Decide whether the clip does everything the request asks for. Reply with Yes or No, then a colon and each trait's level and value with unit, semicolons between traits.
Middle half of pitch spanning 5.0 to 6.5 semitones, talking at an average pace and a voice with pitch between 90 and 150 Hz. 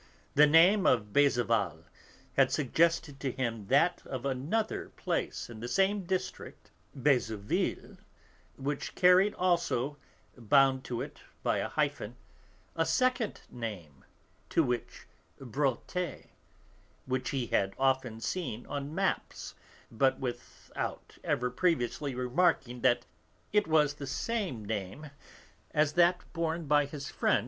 No: wide, 5.5 semitones; slow, 125 wpm; medium, 140 Hz